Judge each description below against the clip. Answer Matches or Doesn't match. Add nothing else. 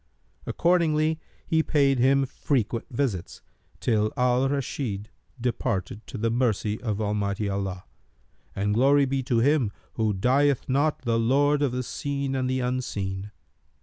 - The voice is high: Doesn't match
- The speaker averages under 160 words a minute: Matches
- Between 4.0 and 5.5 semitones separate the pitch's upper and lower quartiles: Matches